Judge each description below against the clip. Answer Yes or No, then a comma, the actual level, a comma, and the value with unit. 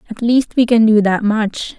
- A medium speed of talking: No, fast, 235 wpm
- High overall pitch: Yes, high, 220 Hz